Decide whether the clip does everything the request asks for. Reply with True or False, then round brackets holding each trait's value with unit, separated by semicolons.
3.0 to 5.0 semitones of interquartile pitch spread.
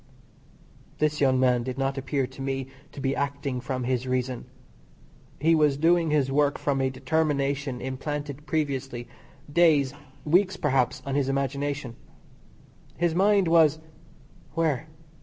False (2.5 semitones)